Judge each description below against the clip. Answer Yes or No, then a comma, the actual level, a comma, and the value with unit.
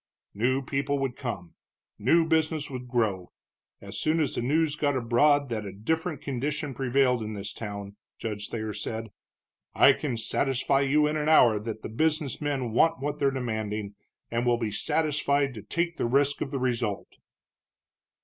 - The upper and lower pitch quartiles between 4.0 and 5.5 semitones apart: Yes, average, 4.8 semitones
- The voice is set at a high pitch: No, low, 130 Hz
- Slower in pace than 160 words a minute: No, average, 170 wpm